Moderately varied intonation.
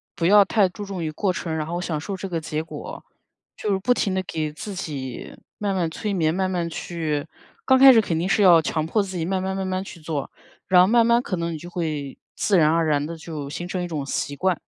Yes: average, 3.4 semitones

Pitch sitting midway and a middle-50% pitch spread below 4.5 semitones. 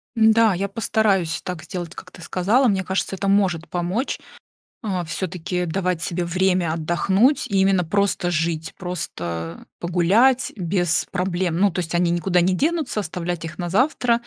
Yes: medium, 180 Hz; narrow, 2.6 semitones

